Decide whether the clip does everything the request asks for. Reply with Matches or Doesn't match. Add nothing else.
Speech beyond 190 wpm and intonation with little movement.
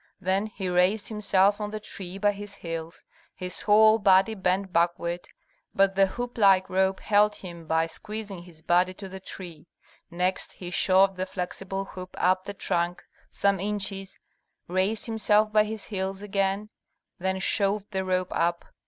Doesn't match